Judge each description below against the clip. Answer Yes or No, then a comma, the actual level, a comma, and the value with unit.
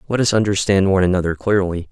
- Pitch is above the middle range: No, very low, 95 Hz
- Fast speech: No, average, 190 wpm